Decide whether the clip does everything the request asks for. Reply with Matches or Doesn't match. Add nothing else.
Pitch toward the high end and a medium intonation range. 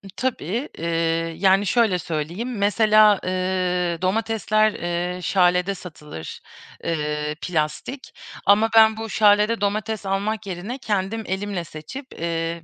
Matches